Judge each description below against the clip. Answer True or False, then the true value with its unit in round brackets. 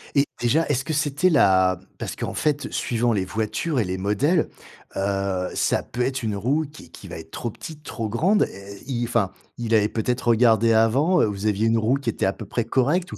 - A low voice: True (115 Hz)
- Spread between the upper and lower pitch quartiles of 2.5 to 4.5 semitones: False (5.1 semitones)